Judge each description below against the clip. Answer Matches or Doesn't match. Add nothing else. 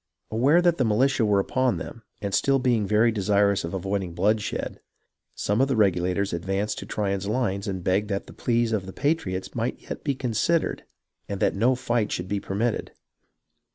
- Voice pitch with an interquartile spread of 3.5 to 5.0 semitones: Matches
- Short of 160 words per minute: Doesn't match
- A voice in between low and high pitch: Doesn't match